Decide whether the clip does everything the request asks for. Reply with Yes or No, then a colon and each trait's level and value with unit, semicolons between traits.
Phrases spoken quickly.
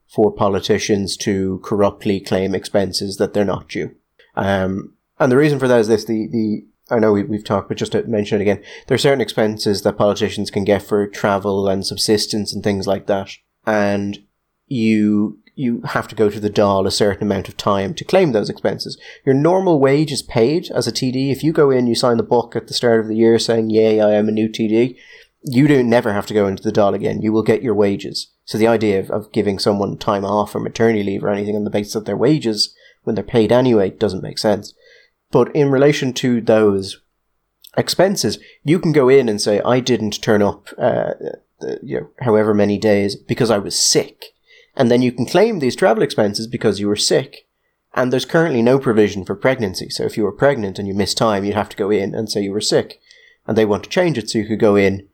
Yes: fast, 230 wpm